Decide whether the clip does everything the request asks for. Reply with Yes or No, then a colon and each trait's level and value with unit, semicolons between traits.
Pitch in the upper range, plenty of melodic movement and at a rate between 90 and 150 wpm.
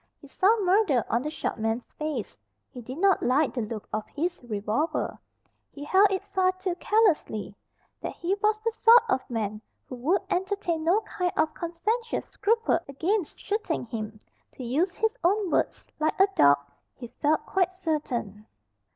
No: very high, 330 Hz; wide, 8.0 semitones; average, 170 wpm